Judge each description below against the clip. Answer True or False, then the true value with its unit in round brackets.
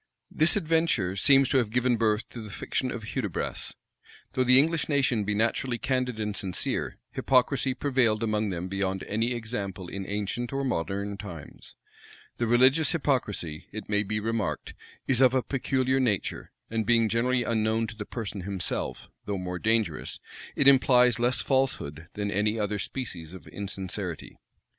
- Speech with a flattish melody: False (4.1 semitones)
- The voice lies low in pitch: True (110 Hz)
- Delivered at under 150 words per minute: False (160 wpm)